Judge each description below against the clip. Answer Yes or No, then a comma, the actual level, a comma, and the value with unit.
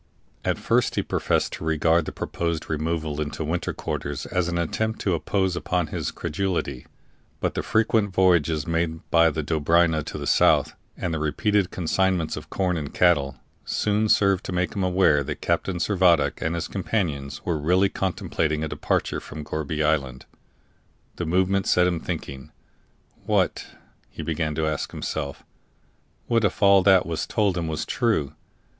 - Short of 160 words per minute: No, average, 165 wpm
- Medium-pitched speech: No, very low, 85 Hz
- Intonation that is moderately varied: Yes, average, 3.4 semitones